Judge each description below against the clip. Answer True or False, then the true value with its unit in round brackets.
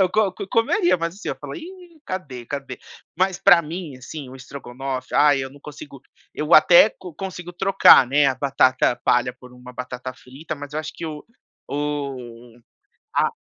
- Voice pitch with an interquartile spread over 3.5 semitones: True (5.6 semitones)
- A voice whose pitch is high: False (145 Hz)